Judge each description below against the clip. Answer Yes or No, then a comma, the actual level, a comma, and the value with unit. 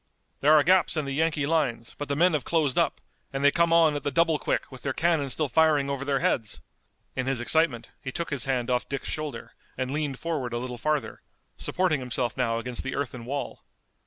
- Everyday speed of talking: No, fast, 220 wpm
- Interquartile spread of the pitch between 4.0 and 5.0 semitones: No, average, 3.6 semitones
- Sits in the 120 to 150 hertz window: Yes, medium, 140 Hz